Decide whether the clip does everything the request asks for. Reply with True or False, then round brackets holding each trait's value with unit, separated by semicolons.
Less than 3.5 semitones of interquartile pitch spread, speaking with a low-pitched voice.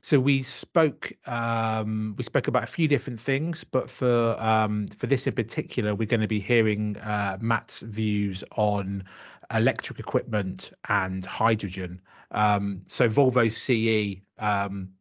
True (3.1 semitones; 110 Hz)